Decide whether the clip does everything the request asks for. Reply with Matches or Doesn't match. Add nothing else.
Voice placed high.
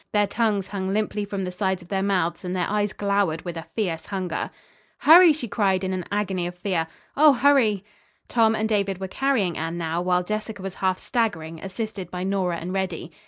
Matches